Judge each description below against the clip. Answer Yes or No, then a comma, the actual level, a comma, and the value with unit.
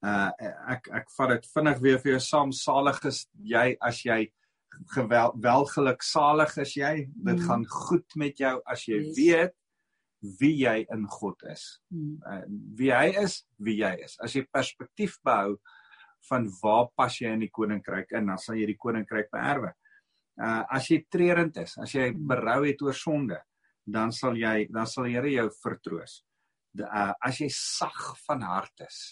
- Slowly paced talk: No, average, 175 wpm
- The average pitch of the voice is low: Yes, low, 130 Hz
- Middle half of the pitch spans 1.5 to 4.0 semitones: No, average, 5.0 semitones